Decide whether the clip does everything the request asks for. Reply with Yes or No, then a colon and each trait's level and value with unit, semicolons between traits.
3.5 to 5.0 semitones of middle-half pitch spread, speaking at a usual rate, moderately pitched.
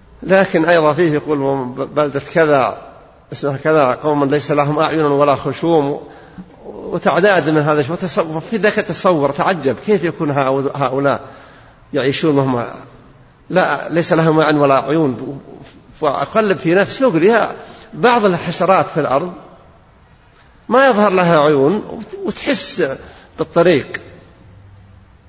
Yes: average, 4.0 semitones; average, 115 wpm; medium, 155 Hz